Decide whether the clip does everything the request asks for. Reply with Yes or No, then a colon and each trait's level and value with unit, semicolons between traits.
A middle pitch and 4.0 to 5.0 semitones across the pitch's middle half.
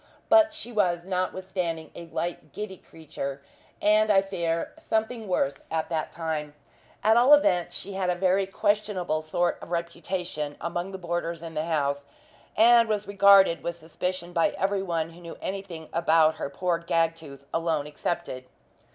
No: medium, 175 Hz; average, 3.2 semitones